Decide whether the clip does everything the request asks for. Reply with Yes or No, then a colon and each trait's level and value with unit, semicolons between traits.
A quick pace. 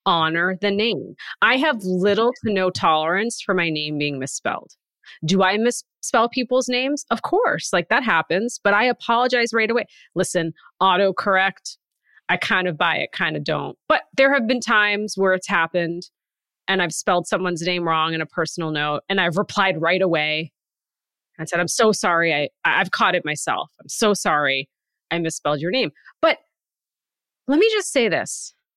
No: average, 175 wpm